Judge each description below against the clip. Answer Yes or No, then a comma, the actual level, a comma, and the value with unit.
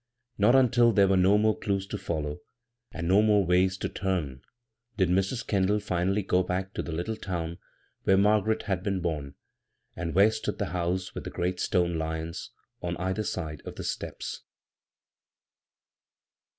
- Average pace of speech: Yes, average, 165 wpm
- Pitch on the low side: Yes, very low, 95 Hz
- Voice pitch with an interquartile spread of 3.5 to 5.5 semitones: No, average, 3.0 semitones